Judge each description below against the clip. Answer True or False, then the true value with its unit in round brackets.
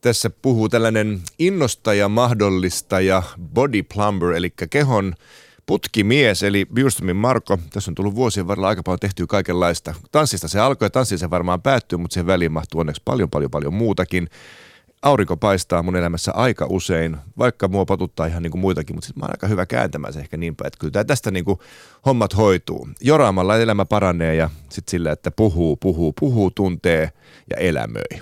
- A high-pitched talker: False (95 Hz)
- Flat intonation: False (3.7 semitones)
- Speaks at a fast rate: True (170 wpm)